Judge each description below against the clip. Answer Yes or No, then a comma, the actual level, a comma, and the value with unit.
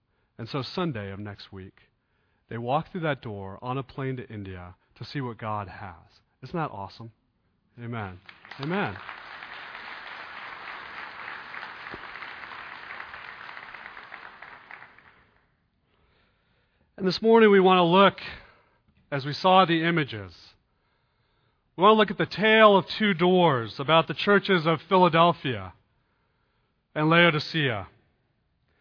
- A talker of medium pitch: No, low, 130 Hz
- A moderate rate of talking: No, slow, 115 wpm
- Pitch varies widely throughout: Yes, wide, 8.5 semitones